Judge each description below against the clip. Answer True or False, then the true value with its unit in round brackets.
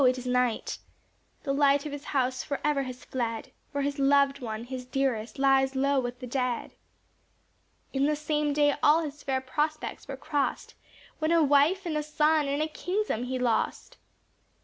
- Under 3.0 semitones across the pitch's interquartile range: True (2.6 semitones)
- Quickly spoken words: False (175 wpm)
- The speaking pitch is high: True (275 Hz)